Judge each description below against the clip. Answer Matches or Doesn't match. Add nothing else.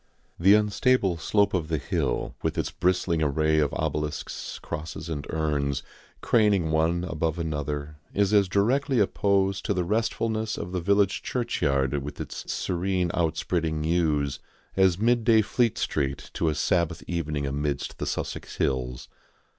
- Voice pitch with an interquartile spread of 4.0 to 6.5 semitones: Matches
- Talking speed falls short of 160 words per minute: Matches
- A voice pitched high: Doesn't match